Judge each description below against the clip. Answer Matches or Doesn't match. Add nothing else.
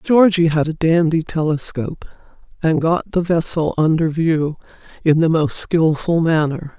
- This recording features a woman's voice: Matches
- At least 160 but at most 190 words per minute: Doesn't match